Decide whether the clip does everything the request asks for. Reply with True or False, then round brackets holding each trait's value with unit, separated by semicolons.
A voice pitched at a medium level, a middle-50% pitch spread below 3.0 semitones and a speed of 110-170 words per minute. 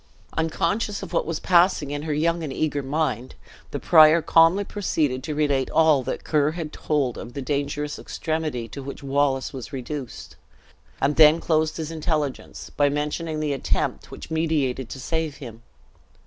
True (150 Hz; 2.6 semitones; 165 wpm)